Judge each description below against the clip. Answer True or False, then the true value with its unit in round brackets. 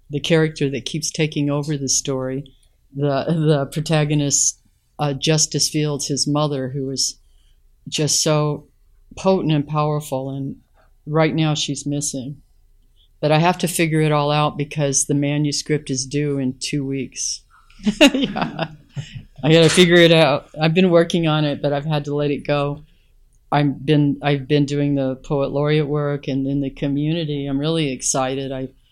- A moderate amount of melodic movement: False (2.0 semitones)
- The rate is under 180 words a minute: True (165 wpm)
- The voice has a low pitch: False (145 Hz)